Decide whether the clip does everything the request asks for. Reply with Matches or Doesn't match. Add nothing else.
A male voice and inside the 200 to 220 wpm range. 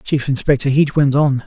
Matches